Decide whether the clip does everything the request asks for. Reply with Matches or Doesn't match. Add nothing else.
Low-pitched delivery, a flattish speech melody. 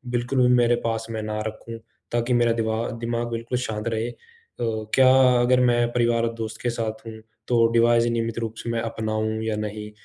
Matches